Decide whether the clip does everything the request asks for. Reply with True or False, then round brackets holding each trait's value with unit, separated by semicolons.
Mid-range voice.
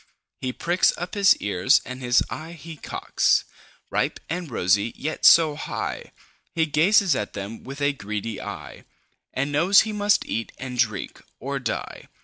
True (145 Hz)